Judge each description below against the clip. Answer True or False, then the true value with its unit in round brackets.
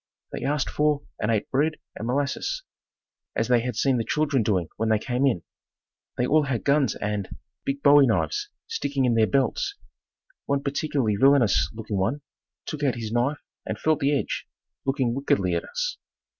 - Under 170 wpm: False (175 wpm)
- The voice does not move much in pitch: False (4.3 semitones)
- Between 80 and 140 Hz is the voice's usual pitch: True (135 Hz)